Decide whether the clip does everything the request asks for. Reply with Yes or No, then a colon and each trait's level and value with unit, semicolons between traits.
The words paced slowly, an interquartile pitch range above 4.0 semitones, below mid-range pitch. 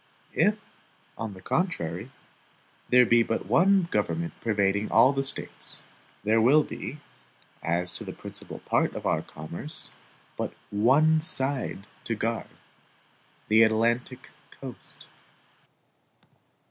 Yes: slow, 115 wpm; average, 5.0 semitones; low, 115 Hz